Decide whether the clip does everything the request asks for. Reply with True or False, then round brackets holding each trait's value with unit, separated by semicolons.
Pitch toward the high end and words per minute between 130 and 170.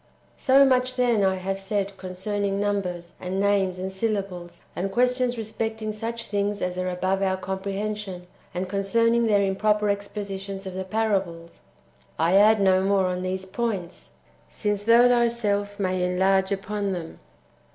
True (200 Hz; 150 wpm)